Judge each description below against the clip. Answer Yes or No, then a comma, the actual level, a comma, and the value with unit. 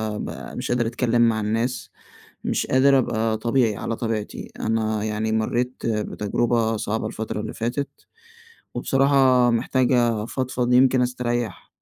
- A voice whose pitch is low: Yes, low, 120 Hz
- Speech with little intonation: Yes, narrow, 2.2 semitones